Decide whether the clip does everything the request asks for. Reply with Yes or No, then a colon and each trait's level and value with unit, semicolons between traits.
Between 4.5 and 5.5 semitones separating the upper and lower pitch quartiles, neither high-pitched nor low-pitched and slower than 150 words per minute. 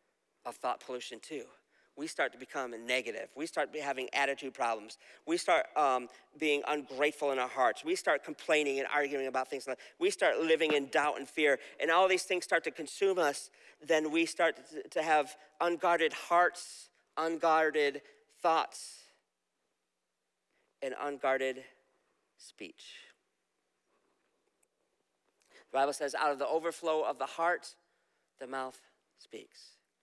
Yes: average, 4.9 semitones; medium, 155 Hz; average, 140 wpm